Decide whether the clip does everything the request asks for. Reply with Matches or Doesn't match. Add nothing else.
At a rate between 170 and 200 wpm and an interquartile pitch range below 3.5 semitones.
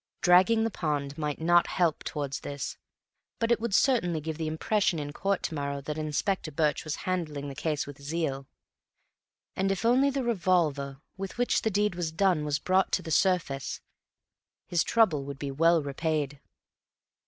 Doesn't match